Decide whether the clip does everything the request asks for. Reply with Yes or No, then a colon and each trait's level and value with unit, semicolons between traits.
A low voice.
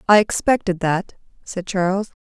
No: high, 190 Hz